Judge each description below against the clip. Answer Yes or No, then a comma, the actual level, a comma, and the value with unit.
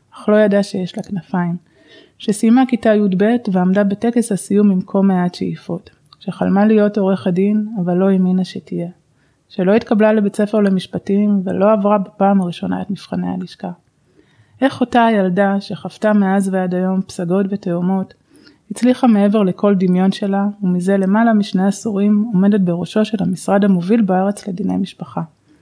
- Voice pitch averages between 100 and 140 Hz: No, high, 195 Hz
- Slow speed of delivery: No, fast, 150 wpm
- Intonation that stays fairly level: Yes, narrow, 2.2 semitones